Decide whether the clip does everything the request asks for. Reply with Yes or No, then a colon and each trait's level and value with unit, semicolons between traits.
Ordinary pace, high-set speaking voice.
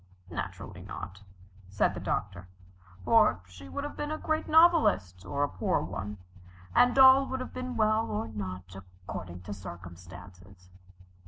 No: average, 150 wpm; very low, 95 Hz